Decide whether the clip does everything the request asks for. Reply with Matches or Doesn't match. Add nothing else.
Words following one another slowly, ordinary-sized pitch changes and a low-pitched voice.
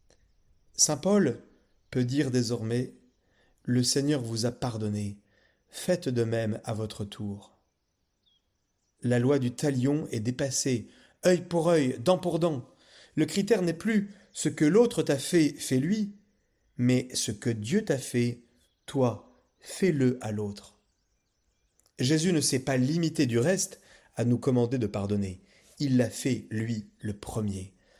Doesn't match